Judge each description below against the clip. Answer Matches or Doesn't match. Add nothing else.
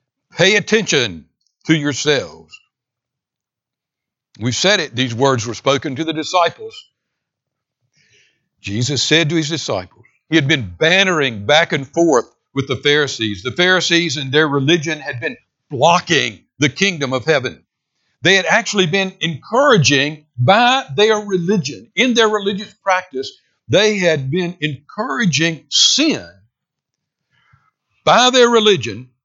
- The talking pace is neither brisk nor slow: Doesn't match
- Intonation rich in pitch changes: Matches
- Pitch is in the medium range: Matches